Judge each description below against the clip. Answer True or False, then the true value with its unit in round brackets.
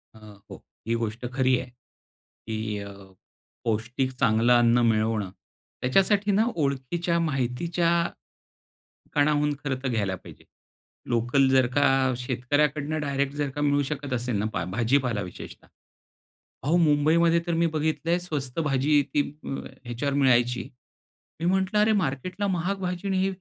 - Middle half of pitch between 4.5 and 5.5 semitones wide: True (5.0 semitones)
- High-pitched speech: False (135 Hz)